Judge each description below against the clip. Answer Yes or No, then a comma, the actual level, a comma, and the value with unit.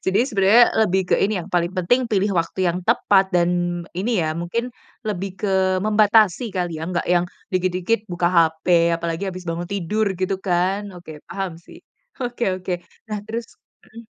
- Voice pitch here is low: No, medium, 185 Hz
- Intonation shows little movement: No, average, 3.1 semitones